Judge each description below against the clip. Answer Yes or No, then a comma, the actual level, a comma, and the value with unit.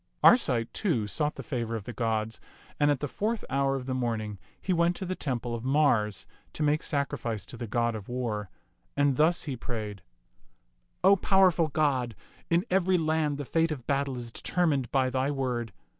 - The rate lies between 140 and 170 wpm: No, average, 190 wpm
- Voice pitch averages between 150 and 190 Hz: No, low, 135 Hz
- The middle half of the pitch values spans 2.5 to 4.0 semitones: No, average, 5.0 semitones